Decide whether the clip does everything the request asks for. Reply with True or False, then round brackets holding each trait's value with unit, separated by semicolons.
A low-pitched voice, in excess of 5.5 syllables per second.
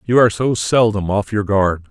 False (105 Hz; 5.1 syllables/s)